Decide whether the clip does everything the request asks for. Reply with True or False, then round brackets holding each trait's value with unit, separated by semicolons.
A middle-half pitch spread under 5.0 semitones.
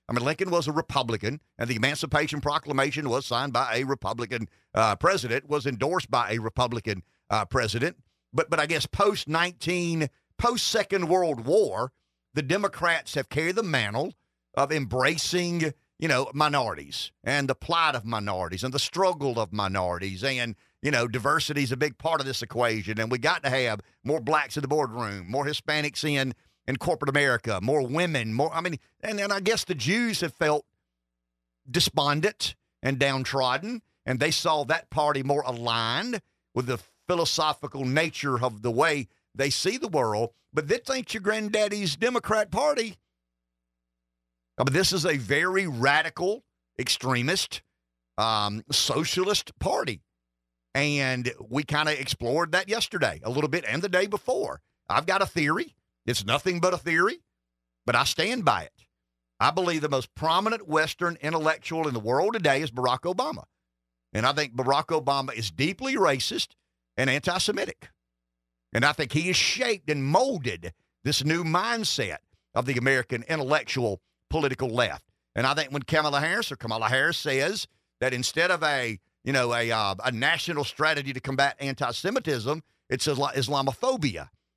False (5.5 semitones)